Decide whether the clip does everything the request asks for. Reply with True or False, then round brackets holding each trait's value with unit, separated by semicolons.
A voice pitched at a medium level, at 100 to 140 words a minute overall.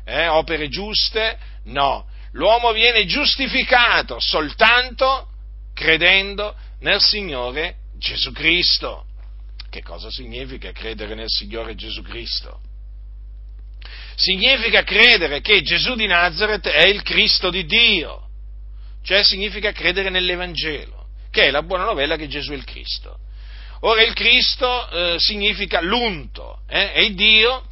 True (175 Hz; 120 wpm)